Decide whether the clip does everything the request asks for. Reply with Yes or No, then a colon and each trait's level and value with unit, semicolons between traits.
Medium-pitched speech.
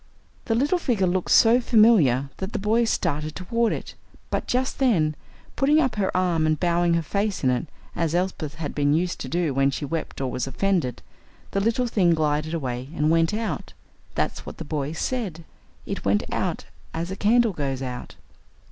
Yes: medium, 170 Hz